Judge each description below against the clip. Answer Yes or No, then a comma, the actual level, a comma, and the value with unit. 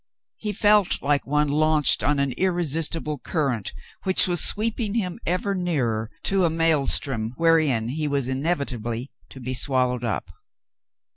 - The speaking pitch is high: No, medium, 150 Hz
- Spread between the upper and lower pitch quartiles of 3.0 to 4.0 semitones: No, average, 5.3 semitones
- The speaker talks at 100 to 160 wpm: Yes, average, 145 wpm